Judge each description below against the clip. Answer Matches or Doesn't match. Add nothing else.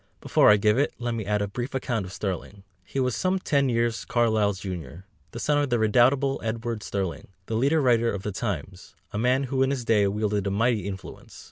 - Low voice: Matches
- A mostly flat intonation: Doesn't match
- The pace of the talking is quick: Matches